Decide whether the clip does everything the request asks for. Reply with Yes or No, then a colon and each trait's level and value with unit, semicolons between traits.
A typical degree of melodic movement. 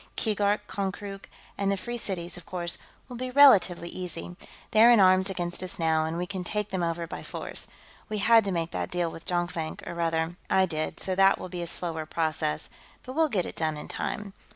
Yes: average, 3.1 semitones